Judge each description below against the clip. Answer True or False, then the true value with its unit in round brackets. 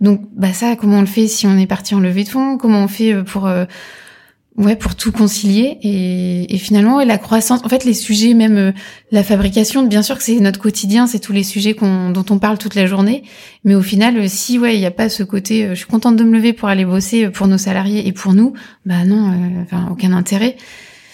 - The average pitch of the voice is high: True (210 Hz)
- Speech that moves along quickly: True (250 wpm)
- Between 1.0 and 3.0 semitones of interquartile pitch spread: True (2.6 semitones)